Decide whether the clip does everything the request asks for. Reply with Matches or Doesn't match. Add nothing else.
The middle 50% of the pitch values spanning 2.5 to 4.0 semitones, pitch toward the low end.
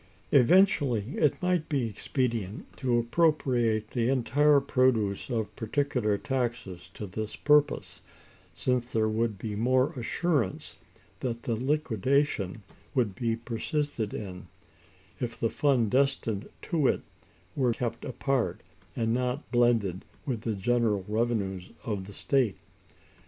Matches